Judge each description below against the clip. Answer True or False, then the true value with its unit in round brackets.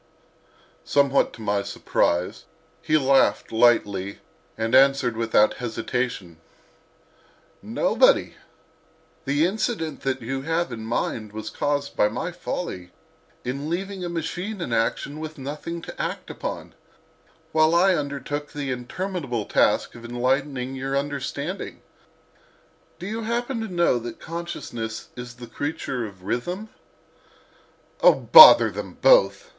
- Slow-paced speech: True (125 wpm)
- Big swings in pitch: True (6.2 semitones)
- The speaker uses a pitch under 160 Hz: True (140 Hz)